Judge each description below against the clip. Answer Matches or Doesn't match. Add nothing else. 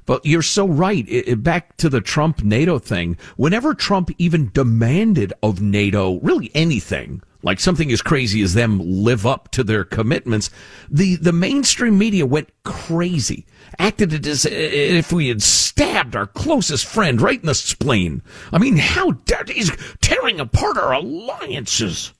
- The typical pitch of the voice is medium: Matches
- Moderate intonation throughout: Doesn't match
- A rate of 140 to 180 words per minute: Matches